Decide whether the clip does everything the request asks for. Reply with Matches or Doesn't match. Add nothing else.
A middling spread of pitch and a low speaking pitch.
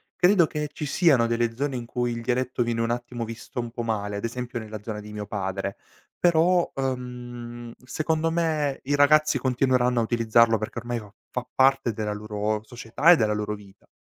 Matches